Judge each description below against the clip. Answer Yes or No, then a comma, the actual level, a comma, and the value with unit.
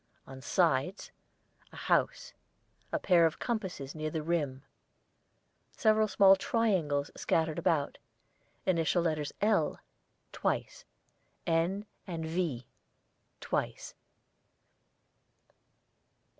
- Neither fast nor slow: No, slow, 90 wpm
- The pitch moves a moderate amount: Yes, average, 4.1 semitones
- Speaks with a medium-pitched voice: Yes, medium, 165 Hz